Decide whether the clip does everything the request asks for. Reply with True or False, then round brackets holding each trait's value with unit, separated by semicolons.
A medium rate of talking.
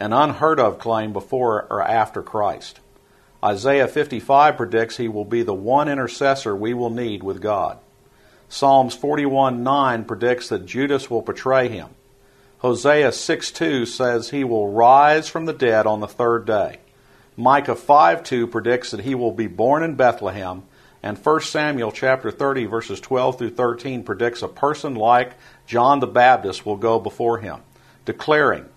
True (155 wpm)